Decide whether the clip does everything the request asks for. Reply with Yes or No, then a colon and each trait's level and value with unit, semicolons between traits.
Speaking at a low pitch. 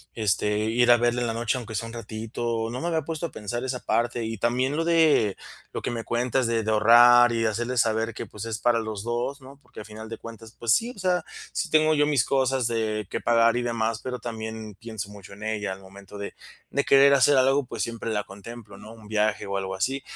Yes: low, 115 Hz